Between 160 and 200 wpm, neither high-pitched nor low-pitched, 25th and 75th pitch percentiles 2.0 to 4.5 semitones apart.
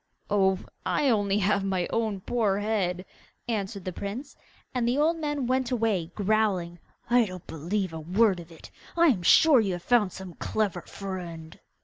No: average, 170 wpm; high, 200 Hz; average, 4.2 semitones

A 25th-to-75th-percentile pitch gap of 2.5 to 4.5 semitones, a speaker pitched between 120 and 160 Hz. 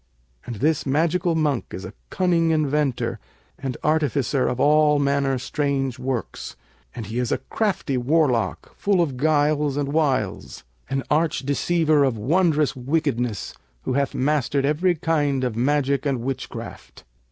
Yes: average, 3.1 semitones; medium, 140 Hz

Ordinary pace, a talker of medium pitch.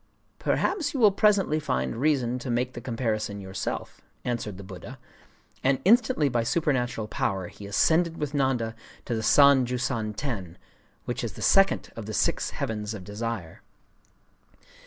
No: average, 150 wpm; low, 120 Hz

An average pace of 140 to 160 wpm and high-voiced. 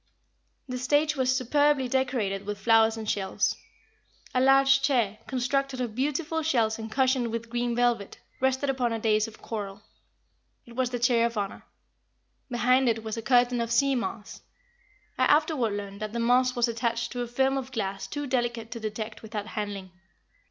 No: average, 175 wpm; high, 240 Hz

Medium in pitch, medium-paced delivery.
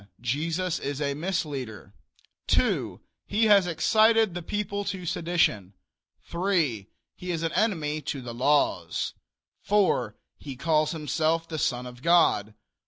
No: medium, 165 Hz; slow, 130 wpm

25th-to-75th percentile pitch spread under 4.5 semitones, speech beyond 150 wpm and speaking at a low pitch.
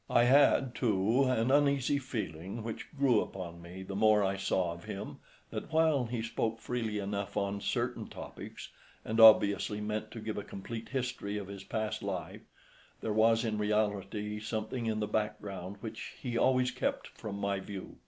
Yes: average, 2.8 semitones; average, 175 wpm; low, 110 Hz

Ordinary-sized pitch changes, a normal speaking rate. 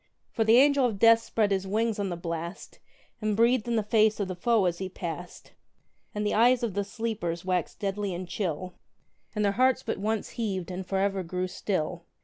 No: average, 3.5 semitones; fast, 210 wpm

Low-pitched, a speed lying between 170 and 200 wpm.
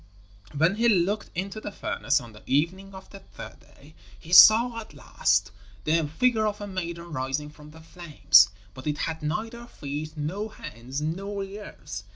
No: medium, 170 Hz; average, 175 wpm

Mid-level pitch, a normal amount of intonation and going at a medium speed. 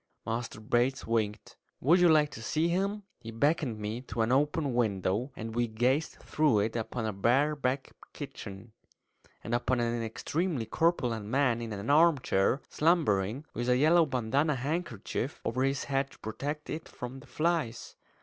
No: low, 125 Hz; average, 4.8 semitones; average, 165 wpm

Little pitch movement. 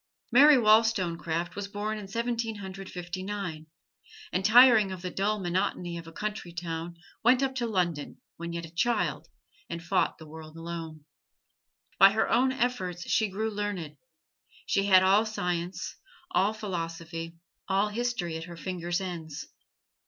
No: average, 4.0 semitones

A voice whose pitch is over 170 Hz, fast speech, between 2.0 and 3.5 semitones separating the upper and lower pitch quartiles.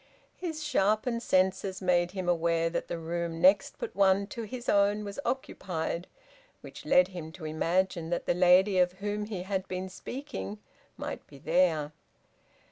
No: medium, 185 Hz; average, 160 wpm; average, 3.2 semitones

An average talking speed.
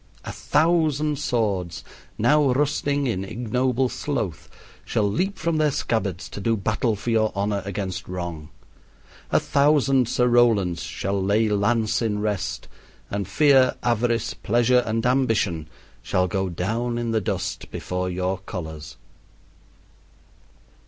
No: slow, 130 wpm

